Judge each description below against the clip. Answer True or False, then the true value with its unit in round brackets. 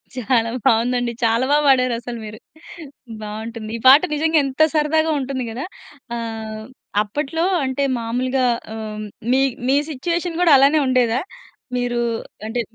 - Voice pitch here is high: True (250 Hz)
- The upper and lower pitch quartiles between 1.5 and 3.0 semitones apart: False (3.6 semitones)